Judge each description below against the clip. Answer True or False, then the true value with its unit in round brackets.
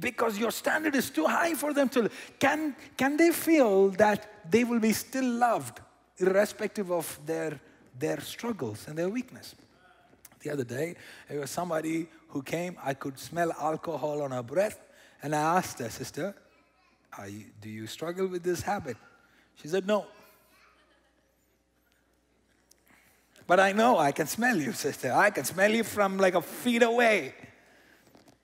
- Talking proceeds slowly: False (160 wpm)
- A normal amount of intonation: False (7.4 semitones)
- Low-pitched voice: False (175 Hz)